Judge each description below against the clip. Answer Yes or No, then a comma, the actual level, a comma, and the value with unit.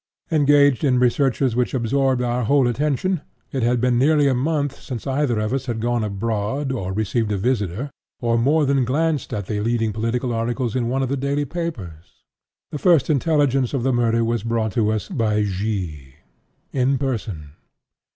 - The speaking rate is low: No, average, 175 wpm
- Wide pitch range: No, average, 3.9 semitones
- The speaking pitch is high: No, low, 125 Hz